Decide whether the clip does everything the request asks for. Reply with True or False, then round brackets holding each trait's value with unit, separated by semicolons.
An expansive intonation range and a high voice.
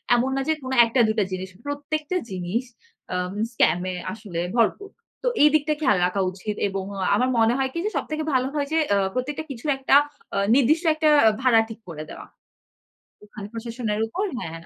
True (6.3 semitones; 235 Hz)